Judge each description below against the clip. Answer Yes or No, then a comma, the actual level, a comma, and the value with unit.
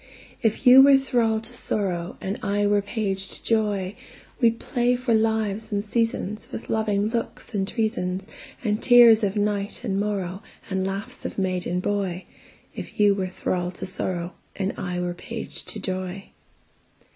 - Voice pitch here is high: Yes, high, 205 Hz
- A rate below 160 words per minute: Yes, average, 140 wpm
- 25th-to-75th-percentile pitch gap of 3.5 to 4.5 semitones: No, average, 2.9 semitones